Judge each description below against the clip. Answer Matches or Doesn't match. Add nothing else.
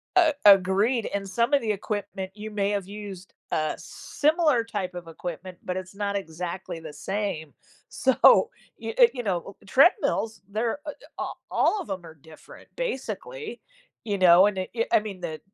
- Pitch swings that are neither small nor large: Matches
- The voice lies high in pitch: Matches